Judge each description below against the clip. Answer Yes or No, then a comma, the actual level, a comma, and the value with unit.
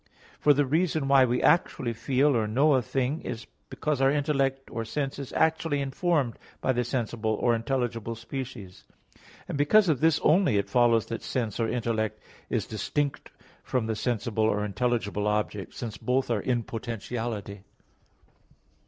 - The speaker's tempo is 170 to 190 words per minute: No, average, 160 wpm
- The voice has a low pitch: Yes, low, 125 Hz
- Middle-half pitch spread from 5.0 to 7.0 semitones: No, average, 3.8 semitones